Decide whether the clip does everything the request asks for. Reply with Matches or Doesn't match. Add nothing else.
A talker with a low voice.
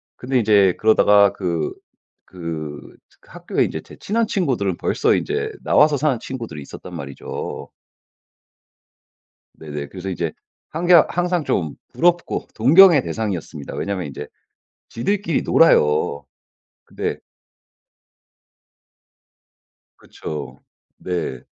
Matches